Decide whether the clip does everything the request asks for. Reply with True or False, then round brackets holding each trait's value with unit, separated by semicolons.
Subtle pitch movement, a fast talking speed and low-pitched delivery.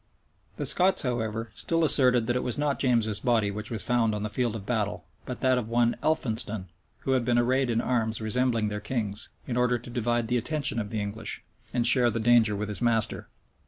True (2.3 semitones; 215 wpm; 120 Hz)